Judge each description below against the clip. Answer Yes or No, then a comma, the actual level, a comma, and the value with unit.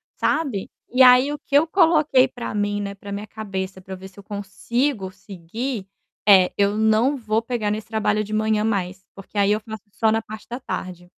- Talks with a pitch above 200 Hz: Yes, high, 215 Hz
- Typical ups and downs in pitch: Yes, average, 3.5 semitones